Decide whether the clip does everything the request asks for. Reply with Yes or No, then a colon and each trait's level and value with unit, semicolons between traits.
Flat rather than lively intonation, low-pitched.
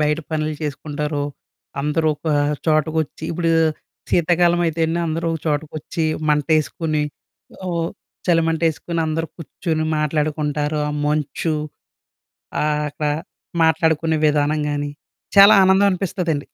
No: narrow, 1.6 semitones; medium, 155 Hz